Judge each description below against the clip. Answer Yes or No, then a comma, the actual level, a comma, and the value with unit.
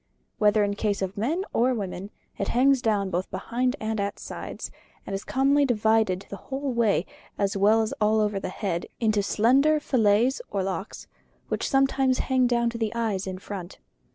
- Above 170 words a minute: Yes, average, 185 wpm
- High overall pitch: Yes, high, 220 Hz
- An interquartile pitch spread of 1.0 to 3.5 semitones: No, average, 4.0 semitones